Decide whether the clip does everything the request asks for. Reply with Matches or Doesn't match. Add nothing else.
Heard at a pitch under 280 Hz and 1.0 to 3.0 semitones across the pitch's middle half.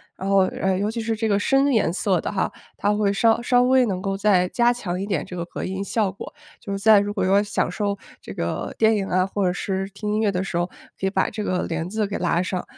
Matches